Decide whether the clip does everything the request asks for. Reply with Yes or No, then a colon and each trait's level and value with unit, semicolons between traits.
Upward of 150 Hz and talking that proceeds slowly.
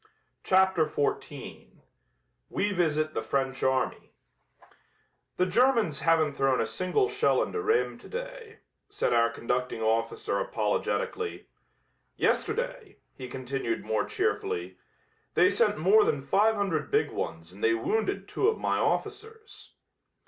Yes: high, 190 Hz; slow, 125 wpm